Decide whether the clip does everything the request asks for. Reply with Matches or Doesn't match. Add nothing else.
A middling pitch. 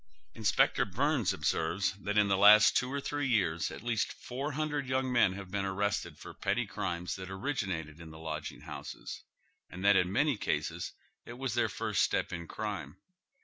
Doesn't match